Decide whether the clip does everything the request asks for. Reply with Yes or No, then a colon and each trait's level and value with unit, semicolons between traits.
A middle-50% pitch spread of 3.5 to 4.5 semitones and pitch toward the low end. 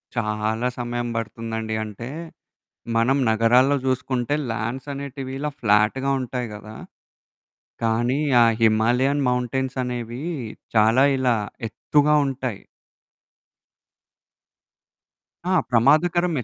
No: average, 3.0 semitones; low, 125 Hz